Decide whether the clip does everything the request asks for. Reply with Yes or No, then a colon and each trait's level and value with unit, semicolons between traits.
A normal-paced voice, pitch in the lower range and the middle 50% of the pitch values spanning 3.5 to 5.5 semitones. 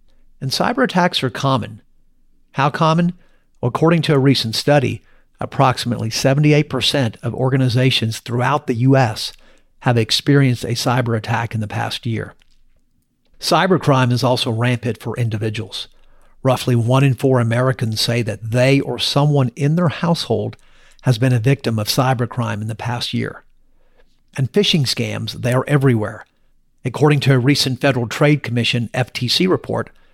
No: average, 145 wpm; low, 125 Hz; average, 2.9 semitones